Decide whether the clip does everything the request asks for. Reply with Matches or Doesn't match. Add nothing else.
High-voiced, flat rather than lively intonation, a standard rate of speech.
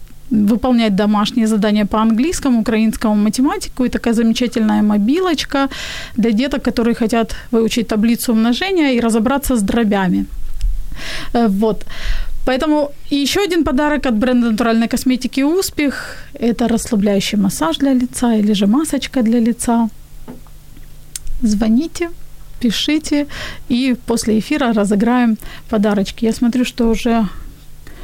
Doesn't match